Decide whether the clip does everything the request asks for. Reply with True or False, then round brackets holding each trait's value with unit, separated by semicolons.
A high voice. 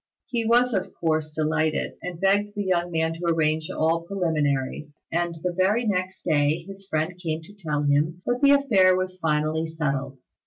False (165 Hz)